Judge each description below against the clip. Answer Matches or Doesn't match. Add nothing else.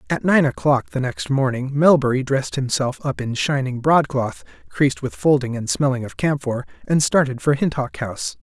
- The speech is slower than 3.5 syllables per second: Doesn't match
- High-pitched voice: Doesn't match